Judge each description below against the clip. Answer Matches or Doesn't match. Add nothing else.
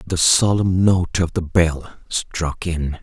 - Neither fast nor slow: Matches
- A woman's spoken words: Doesn't match